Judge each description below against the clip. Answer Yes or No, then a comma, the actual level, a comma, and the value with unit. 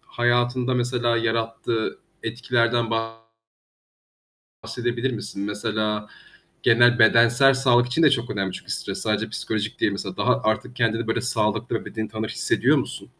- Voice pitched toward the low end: Yes, low, 115 Hz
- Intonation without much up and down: Yes, narrow, 1.9 semitones